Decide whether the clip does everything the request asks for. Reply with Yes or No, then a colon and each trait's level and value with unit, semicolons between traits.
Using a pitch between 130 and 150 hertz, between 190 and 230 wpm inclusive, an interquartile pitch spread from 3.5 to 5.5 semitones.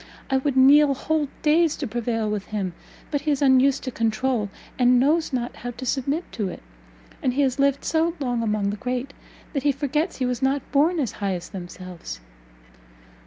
No: very high, 260 Hz; average, 195 wpm; average, 3.9 semitones